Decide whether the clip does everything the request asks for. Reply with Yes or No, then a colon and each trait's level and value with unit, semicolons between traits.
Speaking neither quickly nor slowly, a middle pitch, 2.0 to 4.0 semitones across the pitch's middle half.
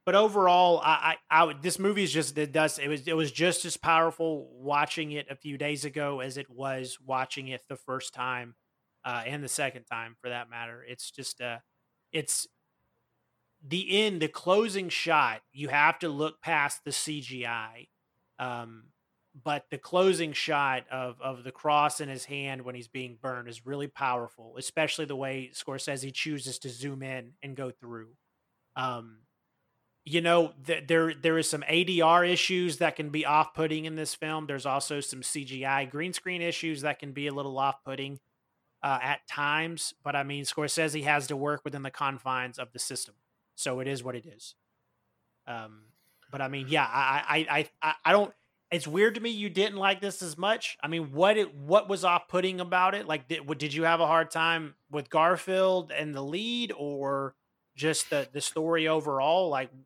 Yes: average, 190 wpm; medium, 145 Hz; average, 3.7 semitones